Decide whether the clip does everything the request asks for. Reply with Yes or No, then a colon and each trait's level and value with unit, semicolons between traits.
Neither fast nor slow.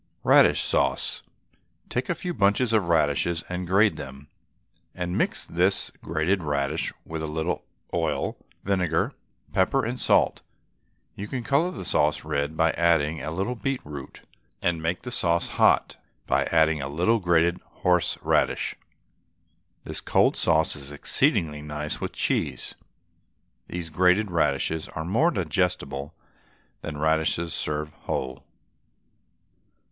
No: slow, 130 wpm